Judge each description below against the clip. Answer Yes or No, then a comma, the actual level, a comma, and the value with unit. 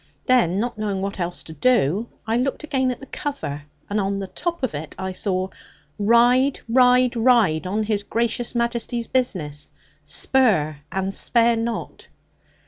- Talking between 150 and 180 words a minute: Yes, average, 155 wpm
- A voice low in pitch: No, high, 225 Hz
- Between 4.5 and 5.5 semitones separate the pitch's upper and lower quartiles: Yes, average, 4.8 semitones